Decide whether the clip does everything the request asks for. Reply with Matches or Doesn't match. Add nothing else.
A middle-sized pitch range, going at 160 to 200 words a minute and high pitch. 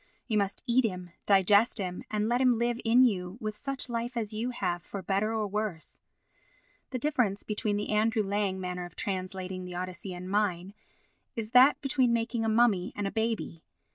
Matches